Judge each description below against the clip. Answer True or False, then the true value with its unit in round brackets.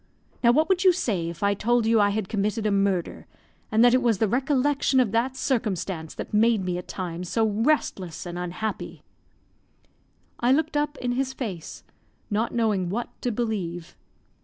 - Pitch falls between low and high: False (220 Hz)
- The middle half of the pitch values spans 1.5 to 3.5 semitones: False (4.6 semitones)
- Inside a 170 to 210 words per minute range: True (180 wpm)